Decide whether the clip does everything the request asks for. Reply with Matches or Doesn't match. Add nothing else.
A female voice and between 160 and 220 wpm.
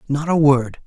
Doesn't match